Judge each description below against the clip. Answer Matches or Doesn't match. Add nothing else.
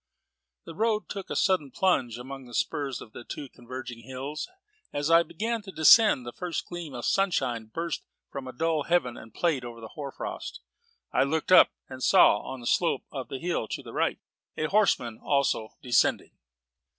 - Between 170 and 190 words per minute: Matches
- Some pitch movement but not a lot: Doesn't match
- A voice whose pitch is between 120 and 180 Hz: Matches